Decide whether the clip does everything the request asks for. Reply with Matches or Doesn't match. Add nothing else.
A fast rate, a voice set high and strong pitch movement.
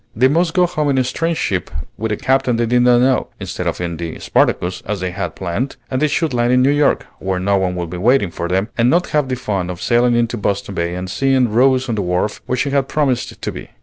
Doesn't match